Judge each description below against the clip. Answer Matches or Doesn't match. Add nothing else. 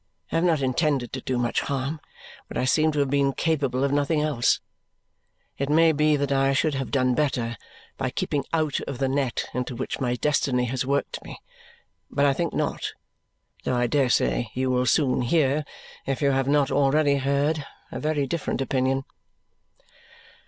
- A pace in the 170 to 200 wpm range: Matches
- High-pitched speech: Doesn't match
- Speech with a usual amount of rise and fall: Doesn't match